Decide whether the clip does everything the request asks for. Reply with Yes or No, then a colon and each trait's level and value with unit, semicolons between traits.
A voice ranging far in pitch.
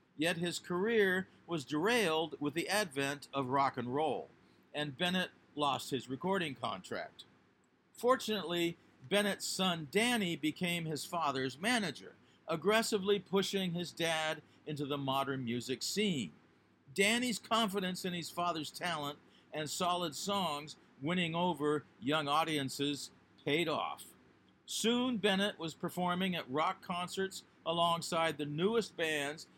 No: average, 4.8 semitones